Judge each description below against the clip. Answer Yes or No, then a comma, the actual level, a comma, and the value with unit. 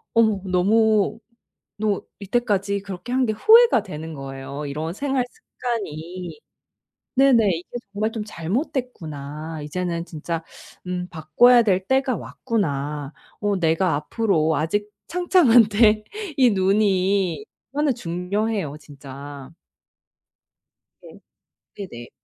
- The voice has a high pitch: Yes, high, 195 Hz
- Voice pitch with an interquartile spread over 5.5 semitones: Yes, wide, 5.9 semitones